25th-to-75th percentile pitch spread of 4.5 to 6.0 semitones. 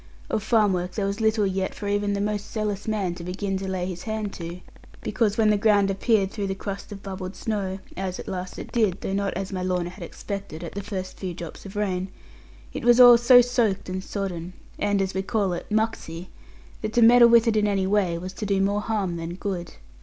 No: narrow, 2.4 semitones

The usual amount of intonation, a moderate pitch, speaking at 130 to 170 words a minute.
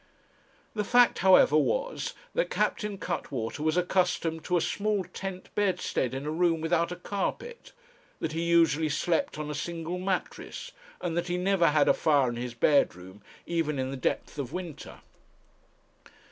Yes: average, 3.8 semitones; medium, 170 Hz; average, 160 wpm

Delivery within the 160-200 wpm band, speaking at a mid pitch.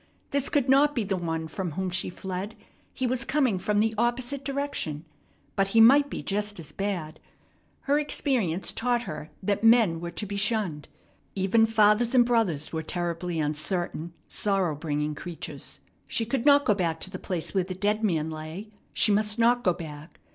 No: average, 185 wpm; high, 200 Hz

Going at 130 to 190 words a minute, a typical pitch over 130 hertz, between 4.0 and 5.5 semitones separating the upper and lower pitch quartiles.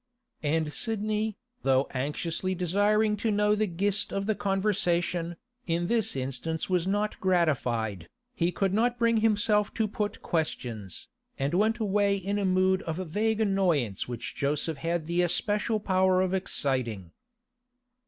Yes: average, 145 wpm; medium, 185 Hz; average, 4.5 semitones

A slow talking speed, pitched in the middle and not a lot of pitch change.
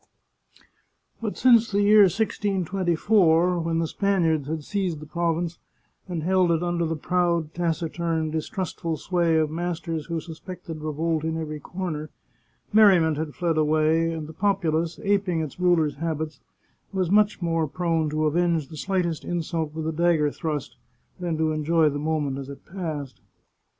No: average, 155 wpm; medium, 165 Hz; narrow, 2.3 semitones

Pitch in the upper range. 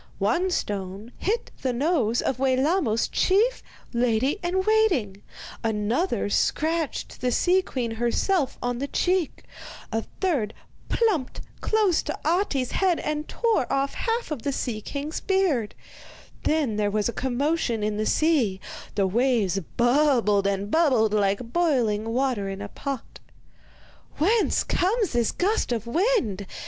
Yes: very high, 260 Hz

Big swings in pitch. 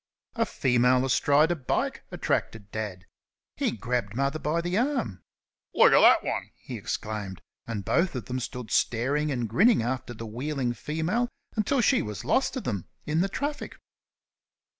Yes: wide, 6.8 semitones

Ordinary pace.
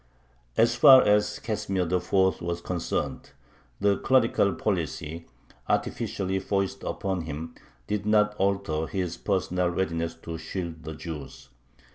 No: slow, 120 wpm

